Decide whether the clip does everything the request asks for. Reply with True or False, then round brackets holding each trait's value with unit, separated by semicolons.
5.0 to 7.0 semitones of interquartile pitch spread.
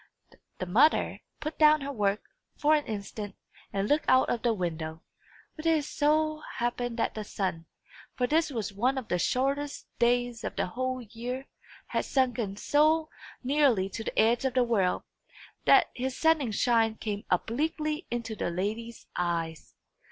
True (5.5 semitones)